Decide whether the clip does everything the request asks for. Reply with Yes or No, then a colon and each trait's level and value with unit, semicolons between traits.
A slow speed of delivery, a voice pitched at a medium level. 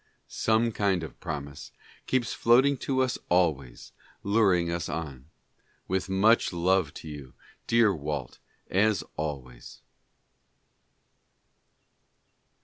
No: slow, 100 wpm; very low, 90 Hz